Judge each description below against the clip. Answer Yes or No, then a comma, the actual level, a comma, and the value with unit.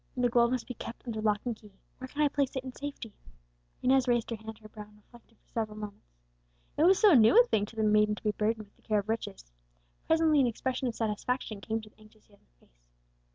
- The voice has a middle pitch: No, high, 225 Hz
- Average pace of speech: No, fast, 250 wpm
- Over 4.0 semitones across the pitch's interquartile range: No, average, 3.2 semitones